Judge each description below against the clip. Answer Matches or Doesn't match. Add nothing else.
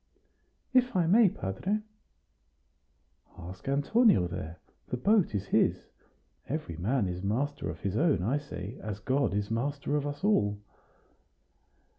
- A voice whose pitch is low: Matches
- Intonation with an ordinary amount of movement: Doesn't match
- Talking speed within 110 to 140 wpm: Matches